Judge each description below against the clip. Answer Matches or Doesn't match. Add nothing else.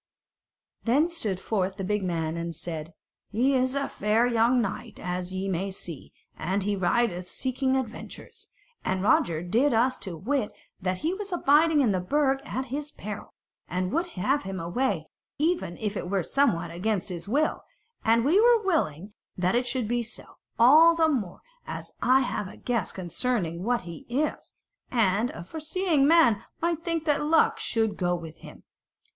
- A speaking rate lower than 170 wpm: Doesn't match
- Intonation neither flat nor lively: Doesn't match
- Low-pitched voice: Doesn't match